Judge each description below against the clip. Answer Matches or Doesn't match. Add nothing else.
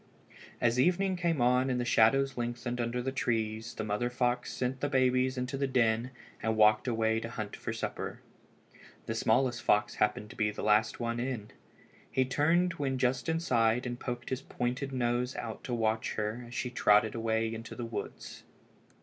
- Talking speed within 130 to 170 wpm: Doesn't match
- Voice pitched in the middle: Doesn't match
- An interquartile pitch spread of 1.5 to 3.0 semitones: Matches